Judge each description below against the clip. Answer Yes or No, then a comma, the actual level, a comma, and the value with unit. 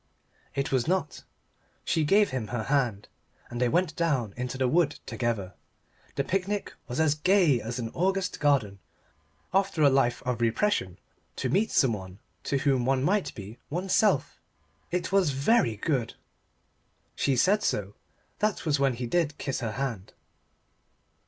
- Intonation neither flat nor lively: No, wide, 6.7 semitones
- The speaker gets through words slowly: No, average, 150 wpm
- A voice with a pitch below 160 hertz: Yes, low, 135 Hz